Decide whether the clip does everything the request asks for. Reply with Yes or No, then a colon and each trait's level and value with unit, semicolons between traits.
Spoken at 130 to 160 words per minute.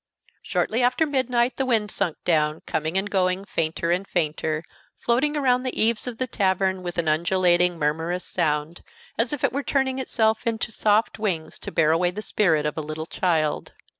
No: average, 185 wpm